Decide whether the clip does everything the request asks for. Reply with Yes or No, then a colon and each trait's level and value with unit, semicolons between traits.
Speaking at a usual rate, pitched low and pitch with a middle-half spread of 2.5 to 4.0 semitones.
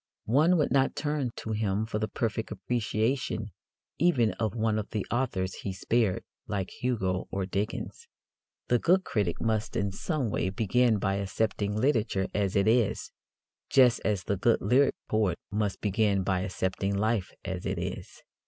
Yes: average, 160 wpm; low, 110 Hz; average, 3.5 semitones